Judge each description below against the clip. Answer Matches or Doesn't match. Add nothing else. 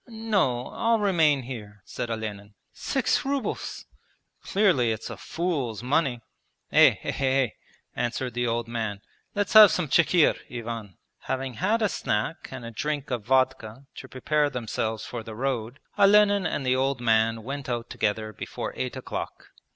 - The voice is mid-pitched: Doesn't match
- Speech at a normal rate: Matches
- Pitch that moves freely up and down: Matches